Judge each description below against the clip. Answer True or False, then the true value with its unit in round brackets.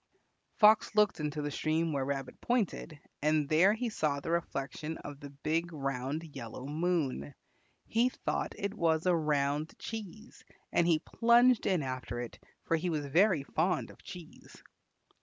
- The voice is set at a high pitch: False (160 Hz)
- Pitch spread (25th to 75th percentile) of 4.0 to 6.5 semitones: True (4.4 semitones)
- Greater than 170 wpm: False (160 wpm)